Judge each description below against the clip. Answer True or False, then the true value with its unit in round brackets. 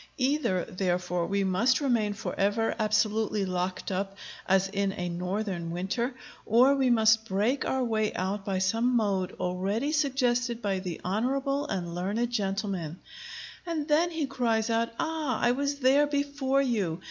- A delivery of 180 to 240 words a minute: False (150 wpm)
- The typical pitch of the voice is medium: False (220 Hz)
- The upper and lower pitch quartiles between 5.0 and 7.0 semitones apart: True (5.5 semitones)